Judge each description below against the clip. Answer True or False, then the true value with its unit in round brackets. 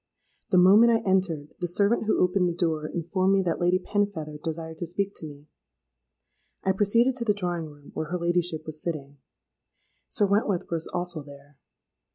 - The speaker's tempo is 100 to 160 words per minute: False (180 wpm)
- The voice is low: False (175 Hz)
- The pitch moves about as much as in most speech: True (3.8 semitones)